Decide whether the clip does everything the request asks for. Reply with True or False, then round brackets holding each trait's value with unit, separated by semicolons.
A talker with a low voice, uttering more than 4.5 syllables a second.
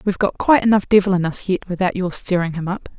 False (190 Hz; 7.0 syllables/s)